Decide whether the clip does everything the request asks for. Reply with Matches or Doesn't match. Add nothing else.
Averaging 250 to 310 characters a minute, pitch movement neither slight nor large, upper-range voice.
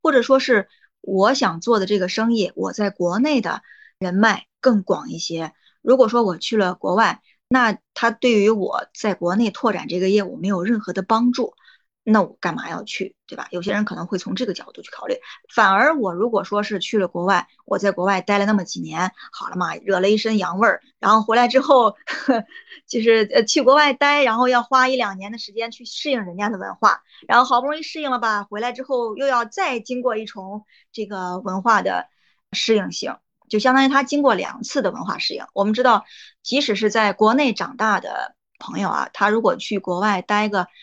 Matches